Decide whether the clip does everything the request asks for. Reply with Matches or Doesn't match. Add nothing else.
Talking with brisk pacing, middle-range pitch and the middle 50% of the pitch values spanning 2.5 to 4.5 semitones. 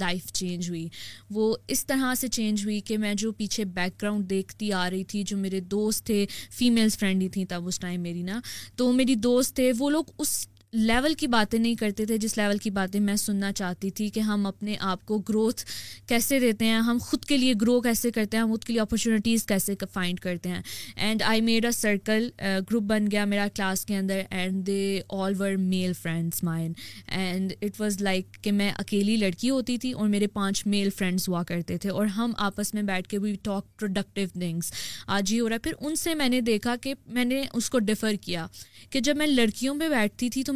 Doesn't match